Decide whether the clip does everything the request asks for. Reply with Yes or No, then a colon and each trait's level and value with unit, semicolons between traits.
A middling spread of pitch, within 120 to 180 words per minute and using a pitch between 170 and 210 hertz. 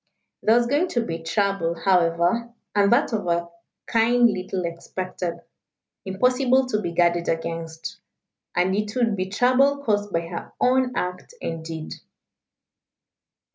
No: wide, 5.8 semitones; slow, 135 wpm; high, 190 Hz